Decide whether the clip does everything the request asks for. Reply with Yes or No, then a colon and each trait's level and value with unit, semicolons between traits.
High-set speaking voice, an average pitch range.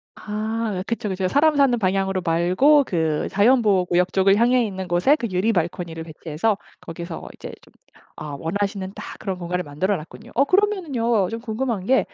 Yes: high, 195 Hz; average, 4.6 semitones